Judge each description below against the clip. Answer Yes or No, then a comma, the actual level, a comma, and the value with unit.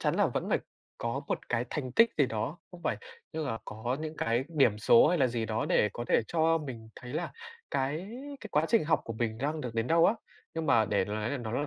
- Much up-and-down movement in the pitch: Yes, wide, 5.7 semitones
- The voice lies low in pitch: Yes, low, 130 Hz